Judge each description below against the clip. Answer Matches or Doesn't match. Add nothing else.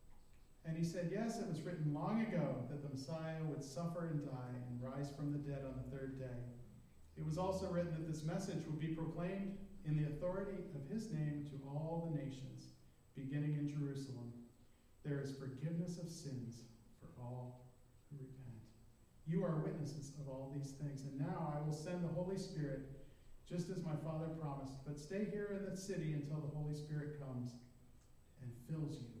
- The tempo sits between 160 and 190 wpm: Matches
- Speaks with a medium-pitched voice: Matches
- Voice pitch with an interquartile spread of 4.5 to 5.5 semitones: Doesn't match